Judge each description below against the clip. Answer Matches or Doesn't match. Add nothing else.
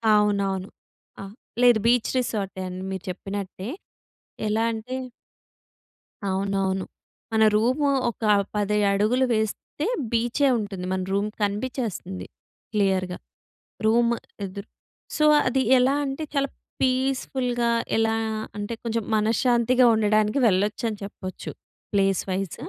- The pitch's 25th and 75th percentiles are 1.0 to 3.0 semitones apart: Doesn't match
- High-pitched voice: Matches